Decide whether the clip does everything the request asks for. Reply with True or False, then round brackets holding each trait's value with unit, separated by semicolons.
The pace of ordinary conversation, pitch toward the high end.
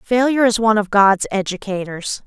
True (160 wpm; 210 Hz)